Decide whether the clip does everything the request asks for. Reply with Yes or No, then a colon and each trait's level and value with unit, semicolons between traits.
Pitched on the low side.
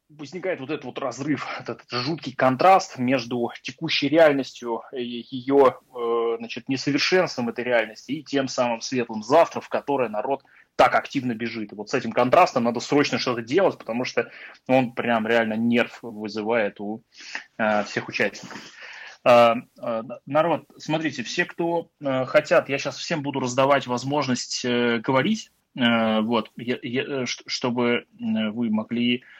Yes: low, 125 Hz